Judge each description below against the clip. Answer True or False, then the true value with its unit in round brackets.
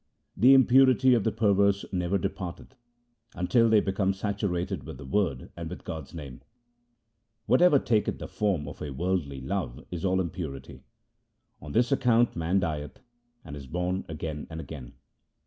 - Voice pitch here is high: False (95 Hz)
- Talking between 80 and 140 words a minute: False (150 wpm)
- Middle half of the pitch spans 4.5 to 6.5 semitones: True (5.0 semitones)